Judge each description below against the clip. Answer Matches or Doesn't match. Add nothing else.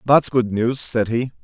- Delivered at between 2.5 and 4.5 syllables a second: Matches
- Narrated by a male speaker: Matches